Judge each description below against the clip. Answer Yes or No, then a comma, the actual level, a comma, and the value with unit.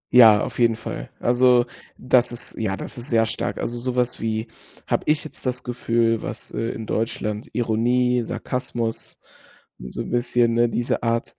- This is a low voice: Yes, low, 120 Hz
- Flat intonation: Yes, narrow, 1.6 semitones